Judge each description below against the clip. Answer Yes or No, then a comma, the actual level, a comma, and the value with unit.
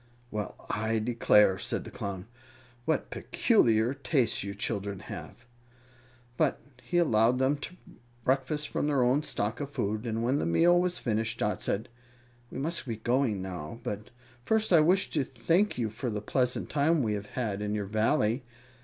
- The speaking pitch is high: No, low, 120 Hz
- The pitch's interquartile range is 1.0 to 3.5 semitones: No, average, 5.1 semitones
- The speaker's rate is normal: Yes, average, 170 wpm